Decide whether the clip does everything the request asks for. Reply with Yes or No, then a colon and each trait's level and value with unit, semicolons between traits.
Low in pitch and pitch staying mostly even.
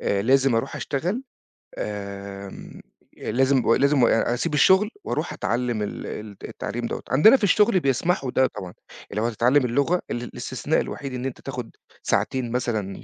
No: low, 125 Hz; average, 3.7 semitones